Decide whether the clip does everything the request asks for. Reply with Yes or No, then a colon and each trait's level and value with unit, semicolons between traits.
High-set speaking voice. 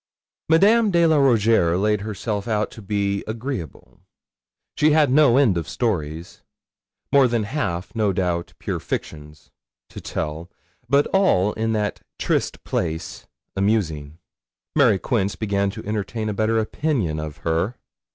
No: low, 105 Hz